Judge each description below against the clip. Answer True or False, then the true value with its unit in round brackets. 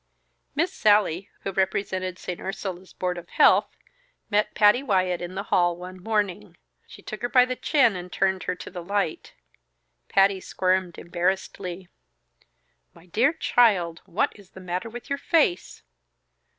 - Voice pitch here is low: False (190 Hz)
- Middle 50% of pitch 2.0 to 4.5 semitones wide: True (2.8 semitones)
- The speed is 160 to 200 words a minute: False (150 wpm)